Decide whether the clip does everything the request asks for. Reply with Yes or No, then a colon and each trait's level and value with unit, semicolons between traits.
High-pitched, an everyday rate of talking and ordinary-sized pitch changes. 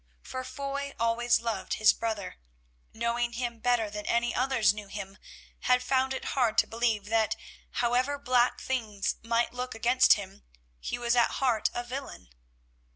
No: high, 240 Hz; average, 160 wpm; narrow, 2.2 semitones